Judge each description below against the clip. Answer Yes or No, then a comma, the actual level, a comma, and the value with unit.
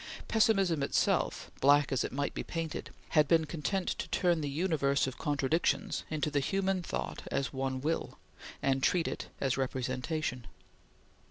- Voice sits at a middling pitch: Yes, medium, 145 Hz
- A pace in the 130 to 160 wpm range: Yes, average, 155 wpm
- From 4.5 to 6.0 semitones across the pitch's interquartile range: No, average, 3.6 semitones